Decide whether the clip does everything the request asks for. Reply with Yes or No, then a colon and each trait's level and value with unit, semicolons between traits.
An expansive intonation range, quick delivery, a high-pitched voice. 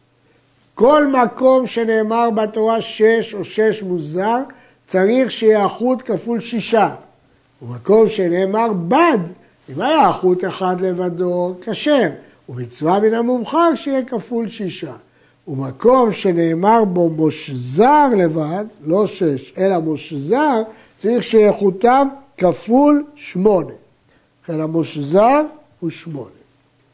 No: wide, 5.8 semitones; slow, 100 wpm; high, 200 Hz